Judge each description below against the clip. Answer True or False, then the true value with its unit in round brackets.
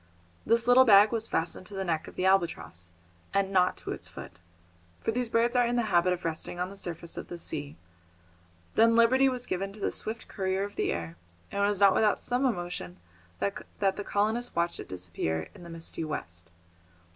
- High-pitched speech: True (195 Hz)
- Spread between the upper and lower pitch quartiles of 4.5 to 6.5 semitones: True (4.9 semitones)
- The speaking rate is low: False (205 wpm)